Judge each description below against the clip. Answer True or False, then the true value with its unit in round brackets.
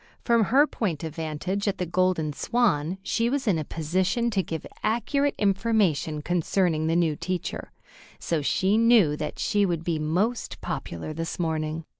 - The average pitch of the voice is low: False (180 Hz)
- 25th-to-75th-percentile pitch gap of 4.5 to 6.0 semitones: True (5.1 semitones)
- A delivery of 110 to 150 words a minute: False (165 wpm)